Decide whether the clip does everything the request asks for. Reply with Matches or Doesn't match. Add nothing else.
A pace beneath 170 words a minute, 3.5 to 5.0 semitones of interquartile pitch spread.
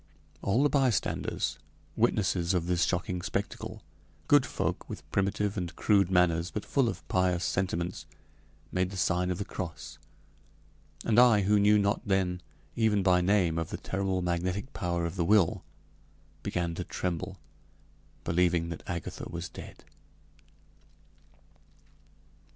Doesn't match